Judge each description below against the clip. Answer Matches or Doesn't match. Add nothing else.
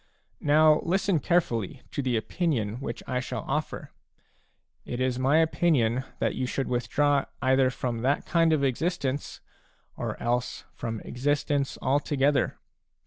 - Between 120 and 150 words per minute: Matches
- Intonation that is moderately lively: Matches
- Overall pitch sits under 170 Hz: Matches